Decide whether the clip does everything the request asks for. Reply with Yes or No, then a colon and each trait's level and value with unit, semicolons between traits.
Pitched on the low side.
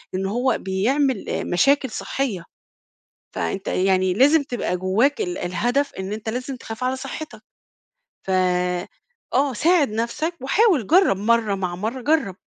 No: high, 235 Hz